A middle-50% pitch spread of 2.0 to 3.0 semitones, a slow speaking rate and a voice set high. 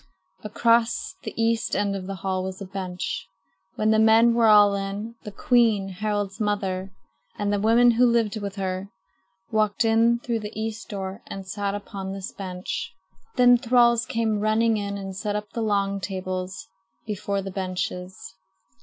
No: narrow, 2.5 semitones; average, 165 wpm; high, 205 Hz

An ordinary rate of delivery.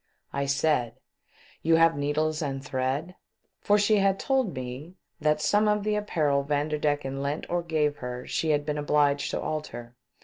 Yes: average, 175 wpm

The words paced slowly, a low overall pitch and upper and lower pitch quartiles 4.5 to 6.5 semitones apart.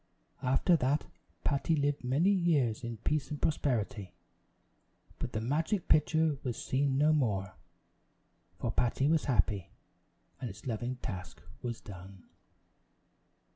Yes: slow, 125 wpm; low, 130 Hz; average, 5.1 semitones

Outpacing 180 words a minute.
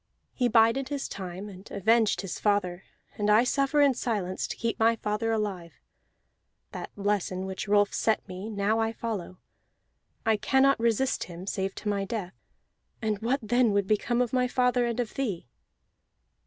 No: average, 170 wpm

